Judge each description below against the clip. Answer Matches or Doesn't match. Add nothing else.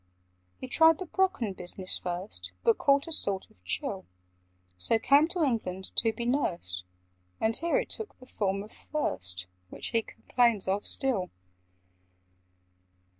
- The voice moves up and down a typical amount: Doesn't match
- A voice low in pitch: Doesn't match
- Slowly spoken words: Doesn't match